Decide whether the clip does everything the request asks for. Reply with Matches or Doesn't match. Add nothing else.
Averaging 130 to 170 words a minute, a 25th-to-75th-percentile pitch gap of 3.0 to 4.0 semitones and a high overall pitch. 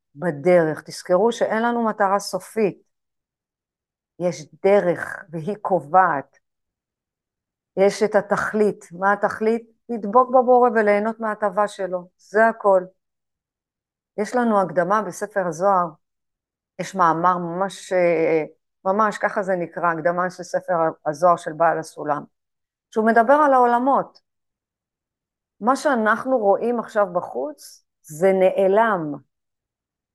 Doesn't match